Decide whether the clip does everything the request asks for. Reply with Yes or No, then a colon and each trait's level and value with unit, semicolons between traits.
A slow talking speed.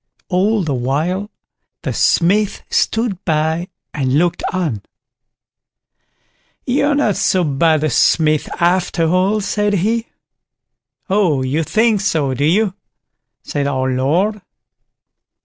Yes: slow, 115 wpm